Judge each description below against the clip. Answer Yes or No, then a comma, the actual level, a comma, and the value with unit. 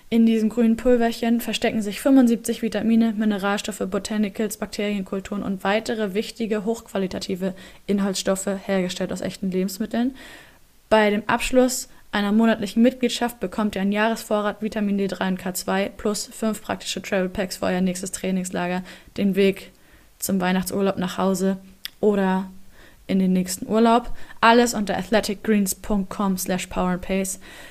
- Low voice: No, high, 205 Hz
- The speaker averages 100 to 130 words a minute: Yes, slow, 125 wpm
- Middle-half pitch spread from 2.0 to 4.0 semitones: Yes, average, 2.8 semitones